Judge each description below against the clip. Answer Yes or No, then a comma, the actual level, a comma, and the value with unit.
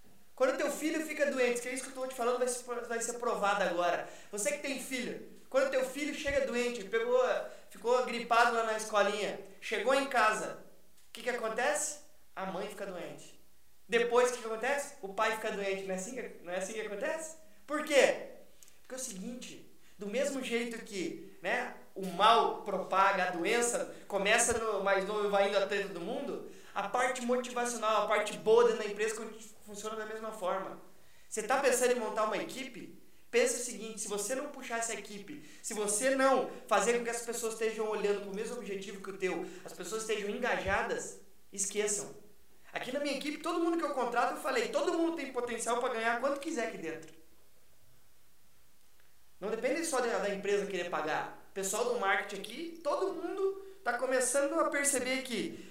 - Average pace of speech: No, fast, 190 wpm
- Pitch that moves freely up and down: No, average, 4.4 semitones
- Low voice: No, high, 230 Hz